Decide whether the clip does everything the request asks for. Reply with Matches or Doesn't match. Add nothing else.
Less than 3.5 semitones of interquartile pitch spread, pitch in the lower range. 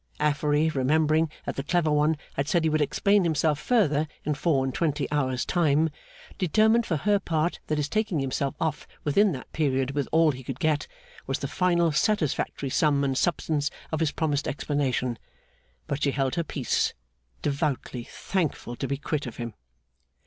Doesn't match